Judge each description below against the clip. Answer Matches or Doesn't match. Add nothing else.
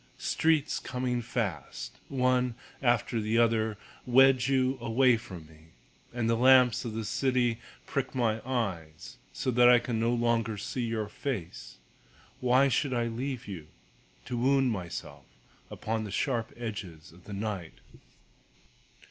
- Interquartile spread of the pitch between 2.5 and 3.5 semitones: Matches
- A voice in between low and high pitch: Doesn't match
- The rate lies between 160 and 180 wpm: Doesn't match